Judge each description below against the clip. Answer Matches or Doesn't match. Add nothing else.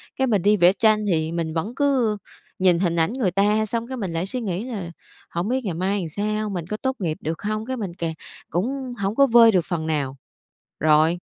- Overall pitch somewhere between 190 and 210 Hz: Matches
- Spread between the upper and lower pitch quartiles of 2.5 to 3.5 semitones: Doesn't match